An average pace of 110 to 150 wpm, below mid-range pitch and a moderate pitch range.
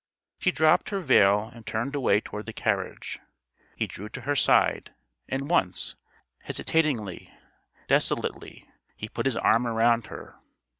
Yes: average, 140 wpm; low, 120 Hz; average, 4.9 semitones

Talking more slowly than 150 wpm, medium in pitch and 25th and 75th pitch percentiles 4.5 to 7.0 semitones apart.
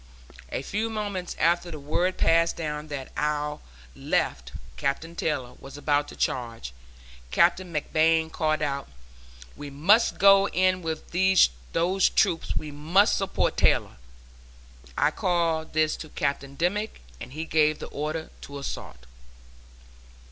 No: slow, 135 wpm; medium, 155 Hz; average, 3.2 semitones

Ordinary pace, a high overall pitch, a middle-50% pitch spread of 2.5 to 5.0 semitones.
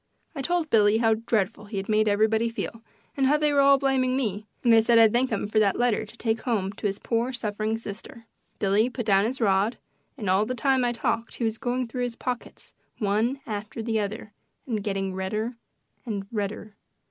No: fast, 210 wpm; high, 225 Hz; average, 2.8 semitones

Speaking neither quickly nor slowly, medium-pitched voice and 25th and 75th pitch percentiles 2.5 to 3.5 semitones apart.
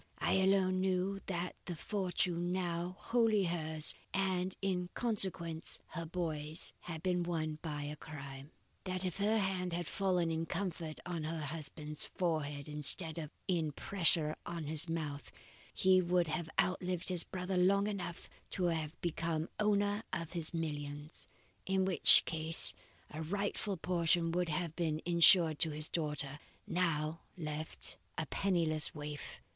Yes: average, 145 wpm; medium, 170 Hz; average, 2.8 semitones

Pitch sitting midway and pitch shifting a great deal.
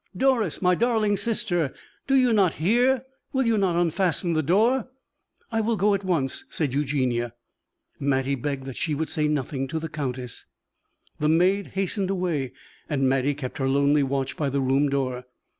Yes: medium, 155 Hz; wide, 6.5 semitones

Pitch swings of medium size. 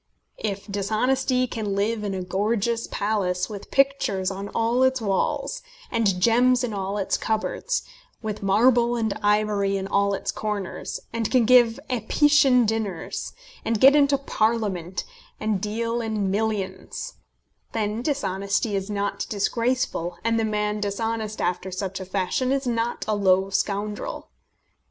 Yes: average, 3.0 semitones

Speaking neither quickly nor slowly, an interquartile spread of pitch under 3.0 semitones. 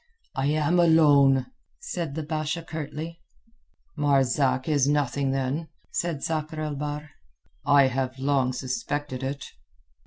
No: slow, 120 wpm; narrow, 2.5 semitones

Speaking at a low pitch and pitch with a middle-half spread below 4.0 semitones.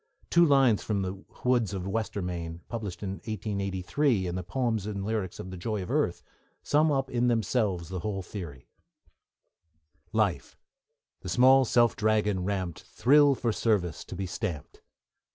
No: low, 105 Hz; average, 4.3 semitones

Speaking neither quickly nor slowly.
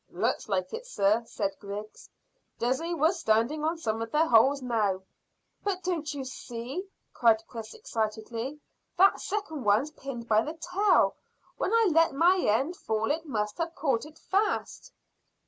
Yes: average, 160 wpm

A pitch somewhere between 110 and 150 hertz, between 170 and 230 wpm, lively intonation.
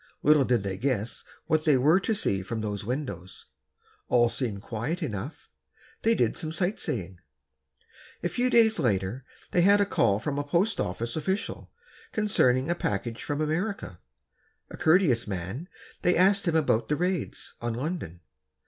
No: medium, 140 Hz; average, 160 wpm; wide, 8.3 semitones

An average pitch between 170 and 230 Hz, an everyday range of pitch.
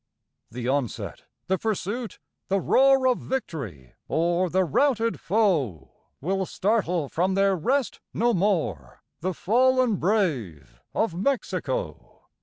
No: high, 190 Hz; wide, 6.8 semitones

